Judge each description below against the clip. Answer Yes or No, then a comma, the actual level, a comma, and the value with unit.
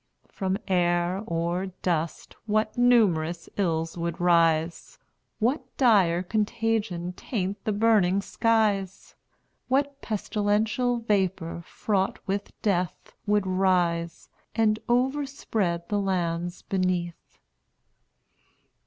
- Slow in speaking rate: Yes, slow, 90 wpm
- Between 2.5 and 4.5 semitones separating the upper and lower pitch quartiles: Yes, average, 3.9 semitones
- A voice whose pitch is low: No, high, 190 Hz